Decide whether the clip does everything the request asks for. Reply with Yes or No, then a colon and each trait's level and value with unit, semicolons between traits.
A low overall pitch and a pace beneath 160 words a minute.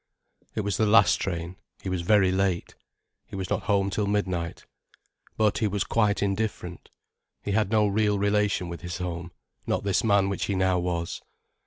No: low, 100 Hz; average, 180 wpm